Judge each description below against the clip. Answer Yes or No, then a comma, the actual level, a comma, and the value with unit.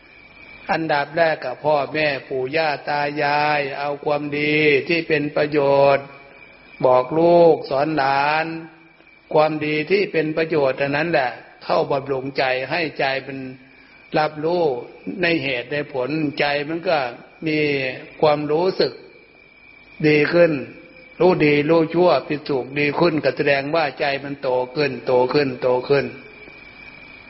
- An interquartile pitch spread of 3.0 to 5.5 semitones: No, narrow, 2.5 semitones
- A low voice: No, medium, 150 Hz